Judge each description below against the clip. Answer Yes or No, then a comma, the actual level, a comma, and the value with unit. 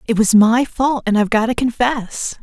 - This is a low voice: No, high, 230 Hz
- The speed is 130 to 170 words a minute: No, fast, 225 wpm